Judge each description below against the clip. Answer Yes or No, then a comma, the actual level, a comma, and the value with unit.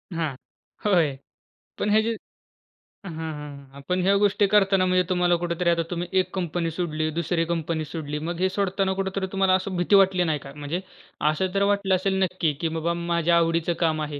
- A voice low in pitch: No, medium, 175 Hz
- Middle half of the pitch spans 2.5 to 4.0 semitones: Yes, average, 2.8 semitones